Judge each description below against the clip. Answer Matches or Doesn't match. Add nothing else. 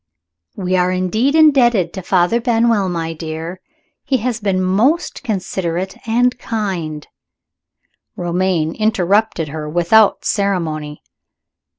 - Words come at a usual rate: Doesn't match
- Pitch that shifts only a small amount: Doesn't match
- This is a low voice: Doesn't match